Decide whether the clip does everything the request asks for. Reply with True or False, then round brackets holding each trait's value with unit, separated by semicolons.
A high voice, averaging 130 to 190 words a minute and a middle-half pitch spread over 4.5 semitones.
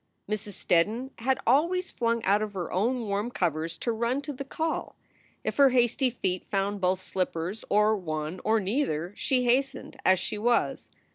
True (215 Hz; 180 wpm; 5.1 semitones)